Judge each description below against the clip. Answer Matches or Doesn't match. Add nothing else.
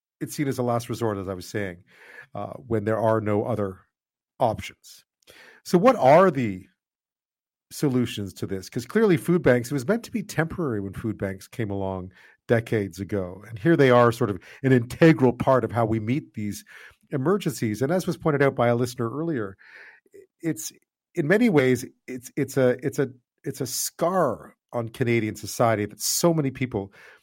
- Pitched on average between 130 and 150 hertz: Doesn't match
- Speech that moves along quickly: Doesn't match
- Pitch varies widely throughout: Matches